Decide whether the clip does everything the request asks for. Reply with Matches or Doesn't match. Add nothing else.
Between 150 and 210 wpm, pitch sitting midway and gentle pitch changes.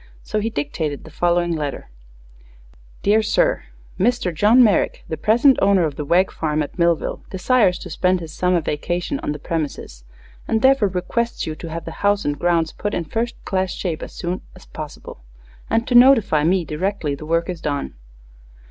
Doesn't match